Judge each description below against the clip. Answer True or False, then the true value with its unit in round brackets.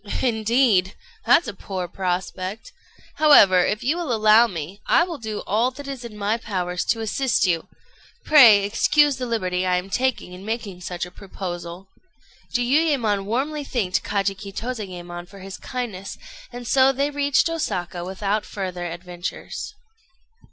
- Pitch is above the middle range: True (210 Hz)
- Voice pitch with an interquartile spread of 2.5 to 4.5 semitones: False (5.4 semitones)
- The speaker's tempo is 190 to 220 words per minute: False (150 wpm)